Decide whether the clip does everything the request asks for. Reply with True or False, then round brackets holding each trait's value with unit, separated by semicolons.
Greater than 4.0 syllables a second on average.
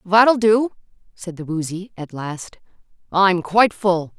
False (3.9 syllables/s)